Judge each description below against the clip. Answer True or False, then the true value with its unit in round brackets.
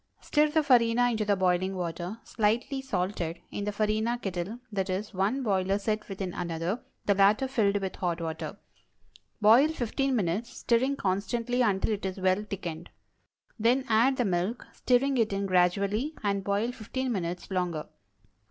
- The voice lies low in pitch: False (205 Hz)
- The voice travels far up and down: False (4.3 semitones)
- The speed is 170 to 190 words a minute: False (160 wpm)